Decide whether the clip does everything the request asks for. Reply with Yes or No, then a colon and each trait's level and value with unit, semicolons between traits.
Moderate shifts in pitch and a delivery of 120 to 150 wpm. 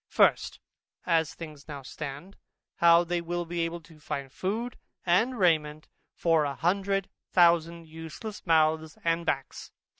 No: narrow, 2.1 semitones; average, 140 wpm